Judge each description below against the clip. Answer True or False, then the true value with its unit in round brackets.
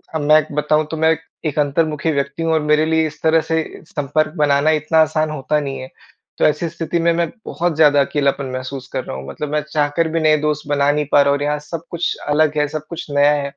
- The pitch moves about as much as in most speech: False (1.7 semitones)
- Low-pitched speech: False (150 Hz)